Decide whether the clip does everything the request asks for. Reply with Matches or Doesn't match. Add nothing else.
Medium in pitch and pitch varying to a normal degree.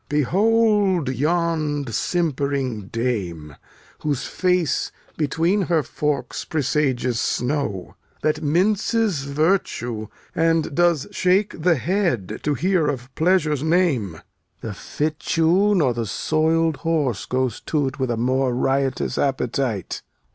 Matches